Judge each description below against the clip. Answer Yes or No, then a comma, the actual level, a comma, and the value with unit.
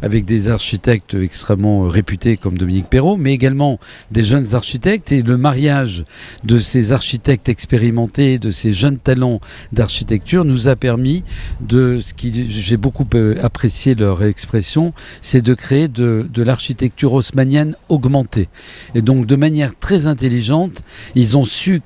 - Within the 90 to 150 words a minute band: Yes, slow, 145 wpm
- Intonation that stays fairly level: No, average, 3.9 semitones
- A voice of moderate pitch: No, low, 125 Hz